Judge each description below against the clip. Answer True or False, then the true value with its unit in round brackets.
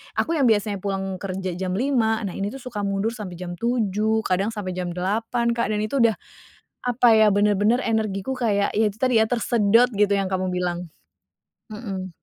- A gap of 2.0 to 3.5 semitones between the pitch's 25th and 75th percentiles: True (3.1 semitones)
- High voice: True (210 Hz)